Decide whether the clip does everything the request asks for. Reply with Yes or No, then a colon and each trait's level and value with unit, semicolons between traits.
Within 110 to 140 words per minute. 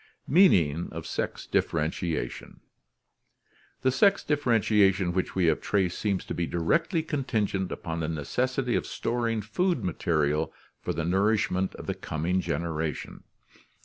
Yes: slow, 135 wpm